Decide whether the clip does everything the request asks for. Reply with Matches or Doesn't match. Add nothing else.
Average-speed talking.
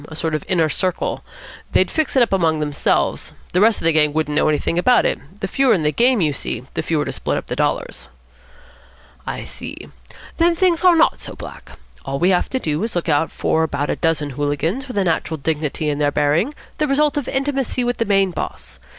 Doesn't match